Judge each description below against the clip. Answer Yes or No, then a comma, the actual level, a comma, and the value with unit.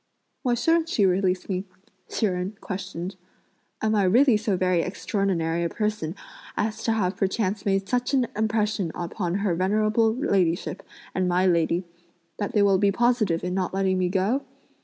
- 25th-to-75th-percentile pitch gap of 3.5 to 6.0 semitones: No, average, 2.9 semitones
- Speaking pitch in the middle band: No, high, 195 Hz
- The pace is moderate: Yes, average, 165 wpm